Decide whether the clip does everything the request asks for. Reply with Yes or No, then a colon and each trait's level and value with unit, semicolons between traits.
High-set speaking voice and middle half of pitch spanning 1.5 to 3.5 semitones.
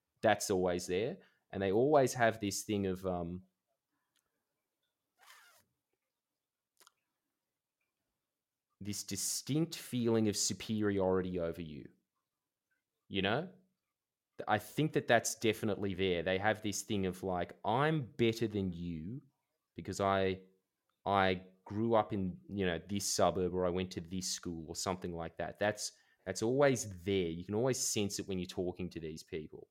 No: low, 100 Hz; average, 3.1 semitones